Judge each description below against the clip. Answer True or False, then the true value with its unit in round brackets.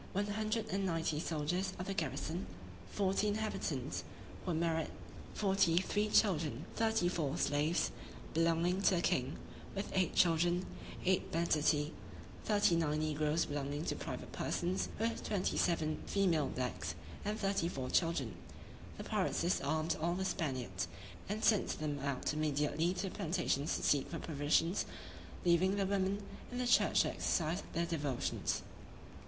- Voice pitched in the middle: True (170 Hz)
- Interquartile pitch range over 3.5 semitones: True (4.2 semitones)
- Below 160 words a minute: True (150 wpm)